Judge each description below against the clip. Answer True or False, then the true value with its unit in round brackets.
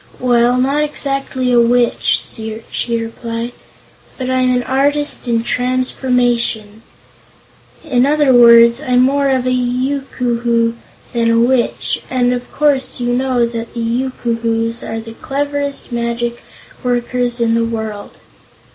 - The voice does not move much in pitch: True (1.8 semitones)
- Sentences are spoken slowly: True (130 wpm)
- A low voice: False (245 Hz)